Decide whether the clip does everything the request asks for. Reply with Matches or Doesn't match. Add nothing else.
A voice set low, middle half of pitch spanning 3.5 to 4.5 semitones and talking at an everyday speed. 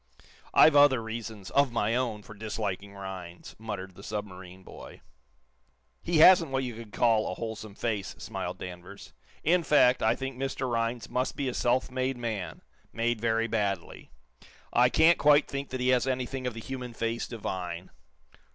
Matches